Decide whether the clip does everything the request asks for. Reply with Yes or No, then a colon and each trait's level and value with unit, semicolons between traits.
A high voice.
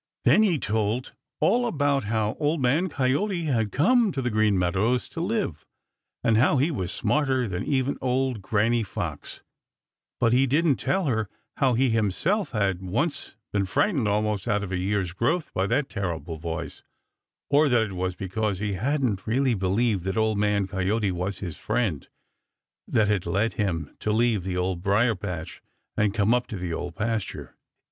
No: low, 110 Hz